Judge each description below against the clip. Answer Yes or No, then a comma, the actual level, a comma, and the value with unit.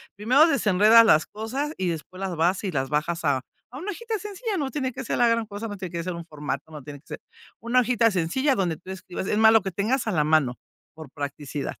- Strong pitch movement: Yes, wide, 7.2 semitones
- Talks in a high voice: Yes, high, 195 Hz